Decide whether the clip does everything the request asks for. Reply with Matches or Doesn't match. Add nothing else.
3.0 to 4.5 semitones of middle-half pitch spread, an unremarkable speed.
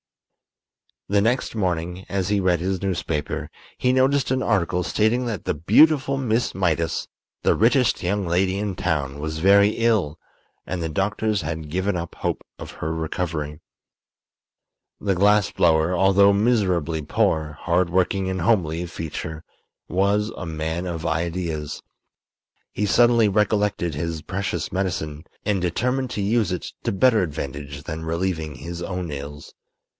Matches